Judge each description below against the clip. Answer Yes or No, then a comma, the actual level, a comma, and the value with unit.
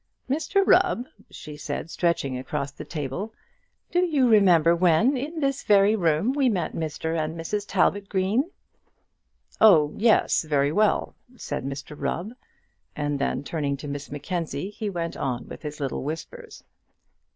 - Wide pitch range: Yes, wide, 6.8 semitones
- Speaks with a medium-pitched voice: Yes, medium, 170 Hz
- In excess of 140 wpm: Yes, average, 150 wpm